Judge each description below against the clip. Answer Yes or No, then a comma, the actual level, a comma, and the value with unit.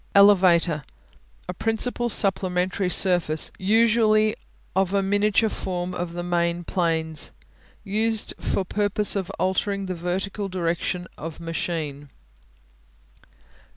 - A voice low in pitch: No, medium, 185 Hz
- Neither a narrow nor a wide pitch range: Yes, average, 3.0 semitones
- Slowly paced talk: Yes, slow, 105 wpm